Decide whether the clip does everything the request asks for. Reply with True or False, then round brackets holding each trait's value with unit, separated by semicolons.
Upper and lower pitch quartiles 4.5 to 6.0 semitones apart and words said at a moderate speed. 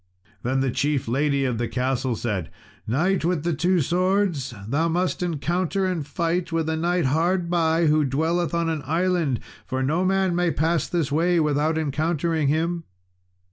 False (3.8 semitones; 170 wpm)